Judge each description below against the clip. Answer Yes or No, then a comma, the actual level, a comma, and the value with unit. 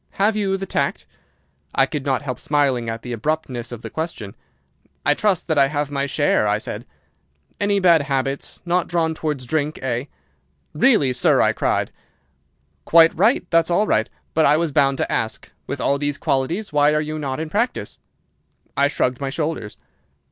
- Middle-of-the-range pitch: Yes, medium, 145 Hz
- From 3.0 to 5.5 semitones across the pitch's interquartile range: Yes, average, 3.6 semitones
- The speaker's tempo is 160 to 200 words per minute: Yes, average, 180 wpm